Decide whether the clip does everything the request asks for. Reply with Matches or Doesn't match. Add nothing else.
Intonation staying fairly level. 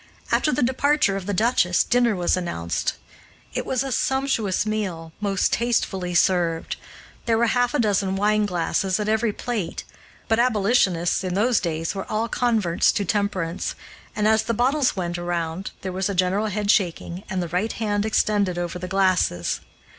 Doesn't match